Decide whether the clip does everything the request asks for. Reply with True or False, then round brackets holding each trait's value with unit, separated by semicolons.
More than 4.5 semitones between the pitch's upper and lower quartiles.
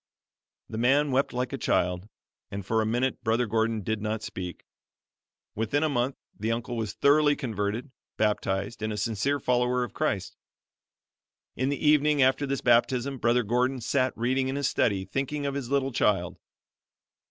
False (3.8 semitones)